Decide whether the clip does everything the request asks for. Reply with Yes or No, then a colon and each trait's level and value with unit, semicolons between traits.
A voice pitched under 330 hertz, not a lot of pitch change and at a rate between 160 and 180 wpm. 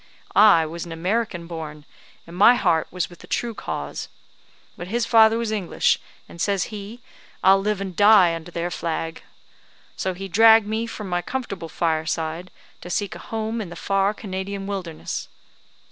No: high, 190 Hz; average, 4.1 semitones; average, 170 wpm